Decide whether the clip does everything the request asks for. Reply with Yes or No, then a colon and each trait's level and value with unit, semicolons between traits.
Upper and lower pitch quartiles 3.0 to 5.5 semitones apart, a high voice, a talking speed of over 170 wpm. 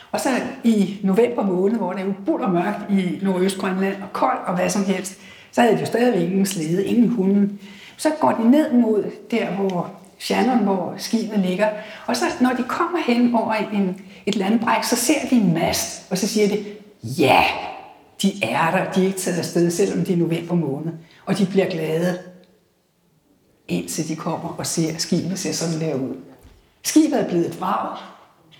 Yes: average, 3.6 semitones; high, 195 Hz; average, 195 wpm